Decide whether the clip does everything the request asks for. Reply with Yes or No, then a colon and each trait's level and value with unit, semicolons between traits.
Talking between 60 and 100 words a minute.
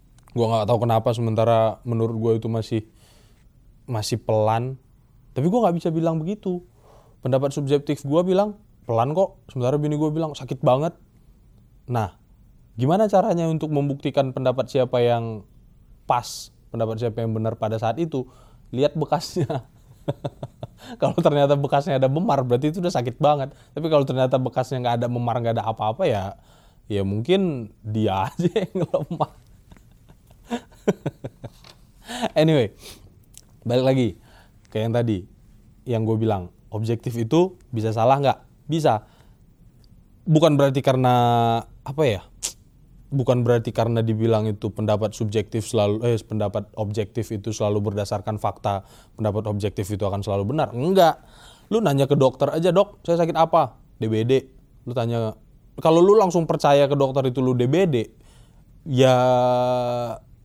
No: average, 135 wpm